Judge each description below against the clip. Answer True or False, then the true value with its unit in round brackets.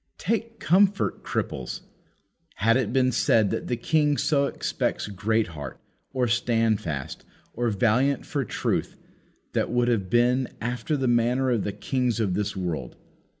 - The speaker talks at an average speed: True (145 wpm)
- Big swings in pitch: False (3.8 semitones)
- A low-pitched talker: True (120 Hz)